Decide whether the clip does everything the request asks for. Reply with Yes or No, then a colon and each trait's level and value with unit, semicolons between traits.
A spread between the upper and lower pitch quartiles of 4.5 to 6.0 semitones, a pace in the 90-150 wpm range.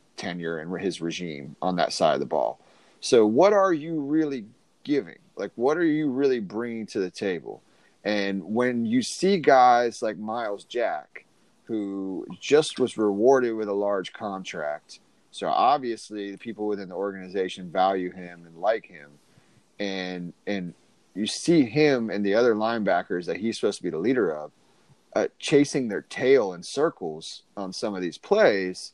No: average, 4.8 semitones; average, 170 wpm